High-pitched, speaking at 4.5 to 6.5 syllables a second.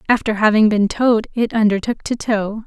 Yes: high, 215 Hz; 5.4 syllables/s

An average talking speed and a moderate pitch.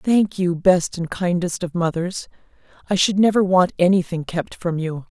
Yes: average, 175 wpm; medium, 180 Hz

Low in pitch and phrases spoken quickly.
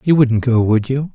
Yes: low, 125 Hz; fast, 260 wpm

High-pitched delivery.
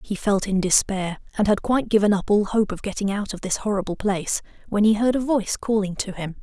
Yes: high, 205 Hz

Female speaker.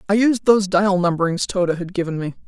Yes: female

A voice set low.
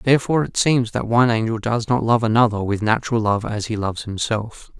Yes: low, 115 Hz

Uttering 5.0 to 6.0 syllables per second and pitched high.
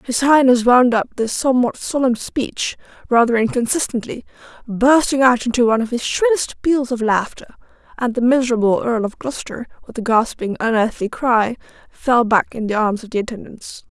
Yes: 5.3 syllables/s; high, 240 Hz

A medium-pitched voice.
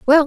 No: very high, 295 Hz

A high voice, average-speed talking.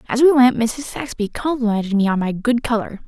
No: high, 235 Hz; fast, 215 wpm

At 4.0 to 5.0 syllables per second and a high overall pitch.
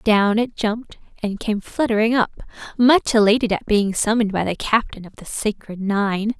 Yes: 4.8 syllables/s; high, 215 Hz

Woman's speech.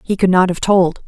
Yes: female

